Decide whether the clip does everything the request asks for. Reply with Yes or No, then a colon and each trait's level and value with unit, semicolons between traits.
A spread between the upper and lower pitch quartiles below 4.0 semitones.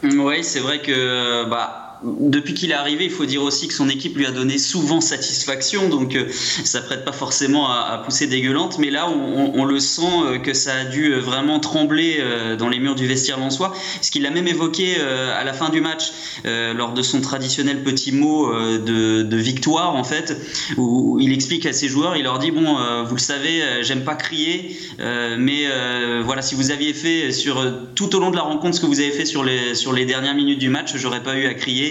Yes: average, 3.0 semitones